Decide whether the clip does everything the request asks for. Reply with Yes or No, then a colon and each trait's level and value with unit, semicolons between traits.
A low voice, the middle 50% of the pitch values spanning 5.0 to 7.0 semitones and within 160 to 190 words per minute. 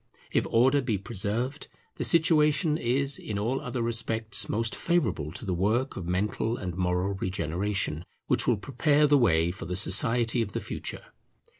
Yes: low, 110 Hz; wide, 5.6 semitones; average, 165 wpm